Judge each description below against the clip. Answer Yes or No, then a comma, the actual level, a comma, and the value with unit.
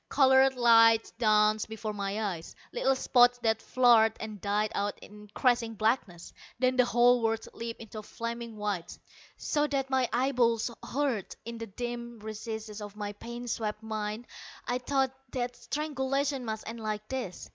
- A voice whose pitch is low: No, high, 230 Hz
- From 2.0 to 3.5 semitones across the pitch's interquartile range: Yes, narrow, 2.6 semitones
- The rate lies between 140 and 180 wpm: Yes, average, 160 wpm